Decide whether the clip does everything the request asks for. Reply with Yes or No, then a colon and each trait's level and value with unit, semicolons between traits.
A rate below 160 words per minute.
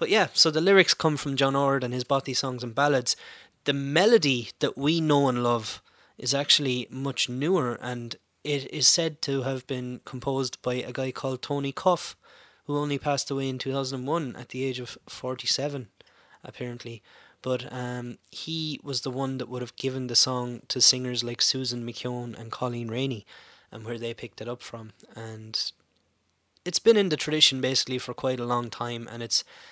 No: average, 190 wpm